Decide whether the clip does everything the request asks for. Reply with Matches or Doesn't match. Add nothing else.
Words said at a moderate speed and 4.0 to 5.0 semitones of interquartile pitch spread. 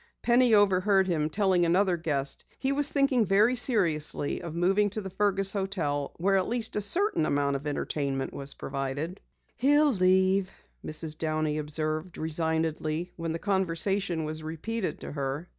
Matches